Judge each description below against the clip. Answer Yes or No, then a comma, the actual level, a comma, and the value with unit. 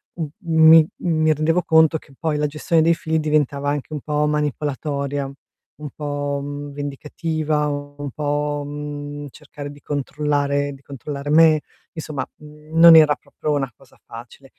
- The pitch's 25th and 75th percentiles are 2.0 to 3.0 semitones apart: No, narrow, 1.4 semitones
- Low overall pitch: No, medium, 150 Hz